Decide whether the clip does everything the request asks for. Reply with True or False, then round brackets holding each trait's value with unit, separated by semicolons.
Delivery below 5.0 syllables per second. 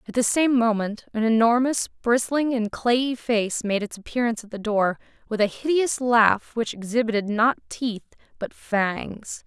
True (4.5 syllables/s)